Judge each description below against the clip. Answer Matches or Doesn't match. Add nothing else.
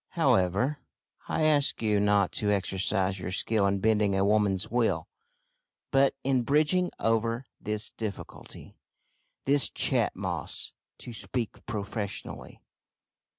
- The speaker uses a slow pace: Matches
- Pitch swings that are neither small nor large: Matches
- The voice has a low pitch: Matches